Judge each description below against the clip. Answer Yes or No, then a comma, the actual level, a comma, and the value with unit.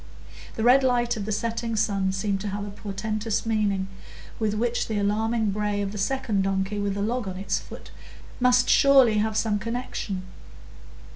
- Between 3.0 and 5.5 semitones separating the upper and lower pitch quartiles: No, narrow, 2.4 semitones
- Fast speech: No, average, 175 wpm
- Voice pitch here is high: Yes, high, 210 Hz